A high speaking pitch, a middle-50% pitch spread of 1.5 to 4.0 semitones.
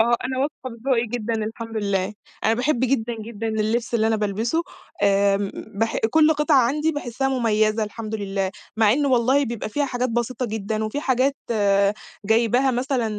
Yes: high, 230 Hz; average, 3.2 semitones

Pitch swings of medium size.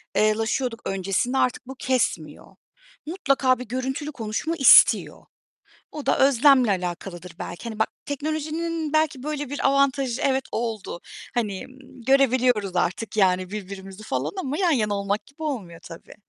No: wide, 5.7 semitones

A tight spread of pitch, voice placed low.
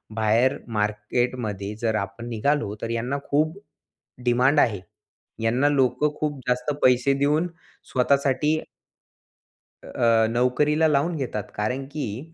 No: average, 4.3 semitones; low, 125 Hz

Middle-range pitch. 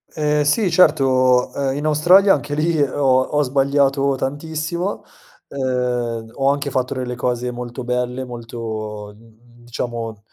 No: low, 130 Hz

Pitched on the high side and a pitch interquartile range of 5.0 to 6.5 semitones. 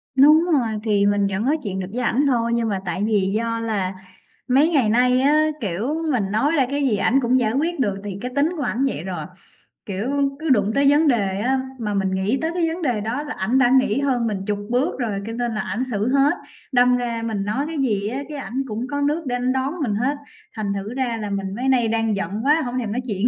No: high, 240 Hz; average, 4.6 semitones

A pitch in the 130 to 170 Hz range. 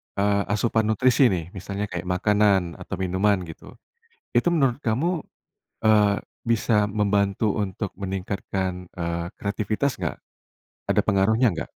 No: low, 100 Hz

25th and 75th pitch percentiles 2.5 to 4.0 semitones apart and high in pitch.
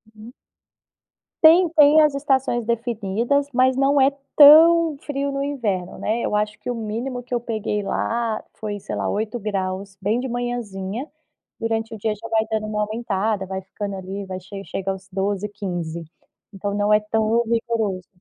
Yes: average, 3.6 semitones; high, 220 Hz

